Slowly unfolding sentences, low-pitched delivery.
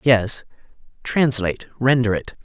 Yes: slow, 100 wpm; low, 120 Hz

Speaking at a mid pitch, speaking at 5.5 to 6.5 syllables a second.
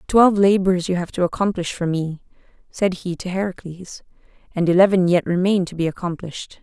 Yes: medium, 180 Hz; 5.6 syllables/s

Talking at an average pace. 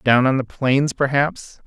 Yes: average, 180 wpm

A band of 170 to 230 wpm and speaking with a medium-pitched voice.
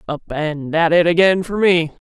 Yes: average, 200 wpm; medium, 170 Hz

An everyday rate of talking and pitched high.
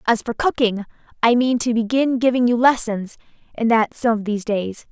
Yes: average, 195 wpm; high, 230 Hz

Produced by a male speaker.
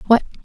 No: female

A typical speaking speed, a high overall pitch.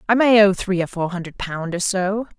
No: fast, 250 wpm; high, 195 Hz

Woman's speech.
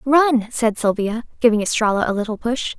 Yes: female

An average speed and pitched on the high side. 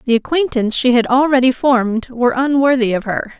Yes: average, 175 wpm; very high, 250 Hz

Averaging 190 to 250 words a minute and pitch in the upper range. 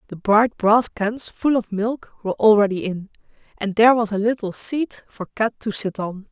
Yes: average, 200 wpm; high, 215 Hz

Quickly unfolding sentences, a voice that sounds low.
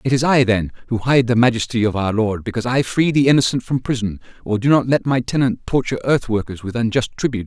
Yes: fast, 240 wpm; low, 120 Hz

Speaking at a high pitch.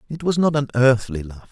No: low, 125 Hz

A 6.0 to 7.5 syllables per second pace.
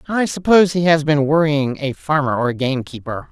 No: 5.7 syllables/s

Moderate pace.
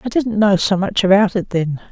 No: fast, 250 wpm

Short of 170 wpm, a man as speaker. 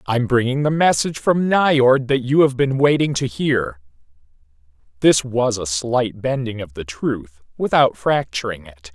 Yes: average, 160 wpm; male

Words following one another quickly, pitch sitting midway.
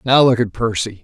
No: fast, 235 wpm; low, 115 Hz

